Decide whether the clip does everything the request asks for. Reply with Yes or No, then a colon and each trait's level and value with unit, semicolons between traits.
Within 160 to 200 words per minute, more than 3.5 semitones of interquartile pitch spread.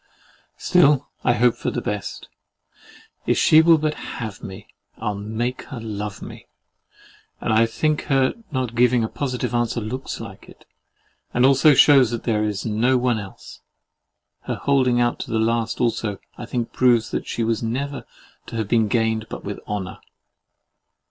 No: average, 170 wpm; average, 2.7 semitones